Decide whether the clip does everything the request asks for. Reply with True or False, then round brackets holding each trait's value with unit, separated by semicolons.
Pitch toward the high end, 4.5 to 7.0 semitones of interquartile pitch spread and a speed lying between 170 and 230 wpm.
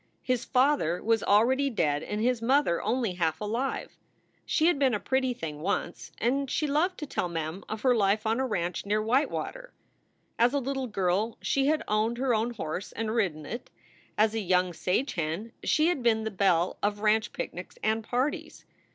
True (225 Hz; 5.1 semitones; 190 wpm)